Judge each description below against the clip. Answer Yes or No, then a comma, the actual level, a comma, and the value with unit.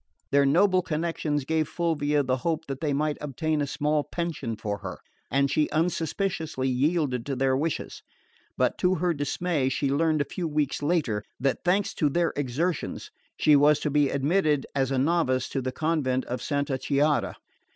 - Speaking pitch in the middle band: Yes, medium, 145 Hz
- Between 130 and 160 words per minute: No, average, 175 wpm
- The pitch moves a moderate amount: Yes, average, 3.2 semitones